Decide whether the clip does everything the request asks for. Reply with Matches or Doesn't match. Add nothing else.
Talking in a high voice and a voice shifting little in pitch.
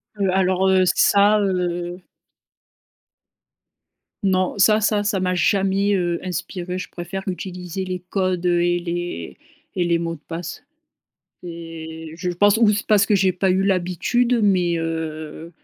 Doesn't match